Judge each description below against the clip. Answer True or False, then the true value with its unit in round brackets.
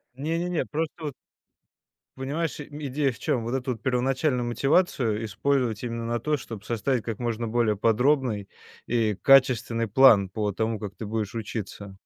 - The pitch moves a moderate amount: True (3.7 semitones)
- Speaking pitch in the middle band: False (120 Hz)